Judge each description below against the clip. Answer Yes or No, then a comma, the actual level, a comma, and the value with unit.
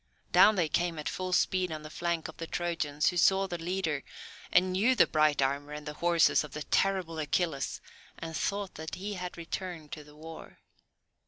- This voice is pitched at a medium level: Yes, medium, 165 Hz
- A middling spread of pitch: Yes, average, 3.1 semitones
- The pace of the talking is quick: No, average, 195 wpm